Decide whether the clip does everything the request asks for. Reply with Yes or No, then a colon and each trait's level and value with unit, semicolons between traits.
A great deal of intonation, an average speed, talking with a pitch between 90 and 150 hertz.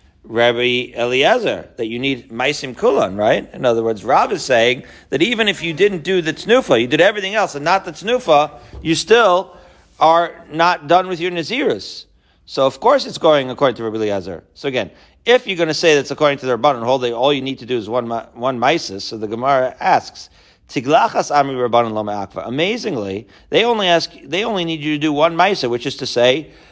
No: wide, 6.6 semitones; fast, 210 wpm; medium, 140 Hz